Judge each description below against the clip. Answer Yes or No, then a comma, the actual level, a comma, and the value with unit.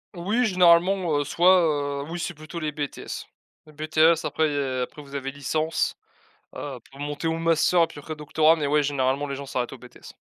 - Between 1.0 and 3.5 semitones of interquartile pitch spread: Yes, average, 2.8 semitones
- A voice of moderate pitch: Yes, medium, 155 Hz